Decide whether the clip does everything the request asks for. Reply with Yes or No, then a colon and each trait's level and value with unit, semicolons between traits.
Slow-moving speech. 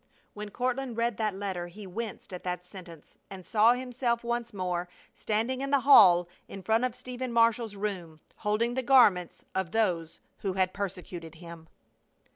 No: average, 160 wpm